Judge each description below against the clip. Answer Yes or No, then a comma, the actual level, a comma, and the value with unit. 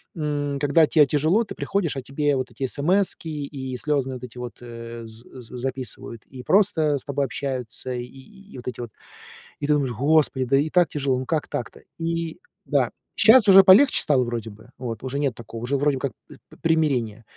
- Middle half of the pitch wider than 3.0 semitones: Yes, average, 3.8 semitones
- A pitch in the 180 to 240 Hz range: No, low, 135 Hz